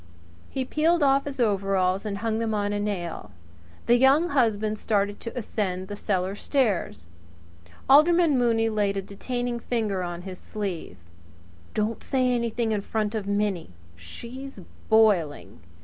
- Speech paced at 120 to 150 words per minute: Yes, average, 145 wpm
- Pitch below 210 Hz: No, high, 215 Hz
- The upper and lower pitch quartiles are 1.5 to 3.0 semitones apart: No, average, 3.8 semitones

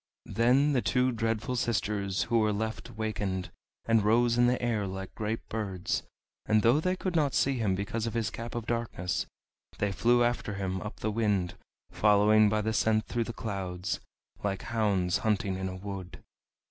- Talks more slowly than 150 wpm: No, average, 180 wpm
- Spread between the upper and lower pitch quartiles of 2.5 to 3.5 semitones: Yes, average, 2.9 semitones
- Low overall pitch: Yes, low, 110 Hz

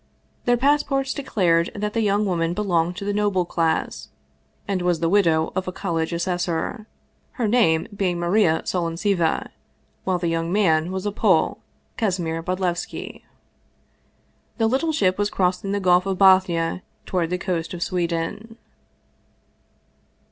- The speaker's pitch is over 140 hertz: Yes, medium, 185 Hz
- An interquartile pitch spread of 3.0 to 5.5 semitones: Yes, average, 3.4 semitones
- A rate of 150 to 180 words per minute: No, average, 140 wpm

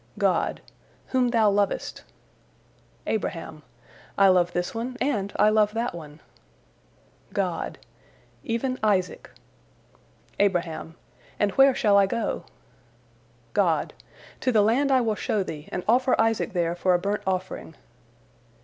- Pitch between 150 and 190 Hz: No, high, 205 Hz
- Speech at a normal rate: No, slow, 125 wpm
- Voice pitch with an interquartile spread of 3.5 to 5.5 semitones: Yes, average, 4.3 semitones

